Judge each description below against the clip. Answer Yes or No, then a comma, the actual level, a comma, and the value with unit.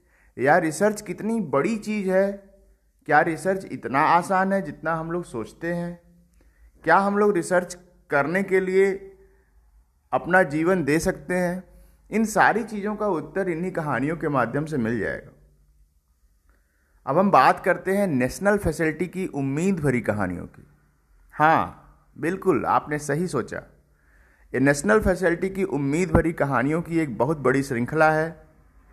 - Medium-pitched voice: Yes, medium, 165 Hz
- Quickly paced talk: No, average, 145 wpm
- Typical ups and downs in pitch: No, wide, 6.8 semitones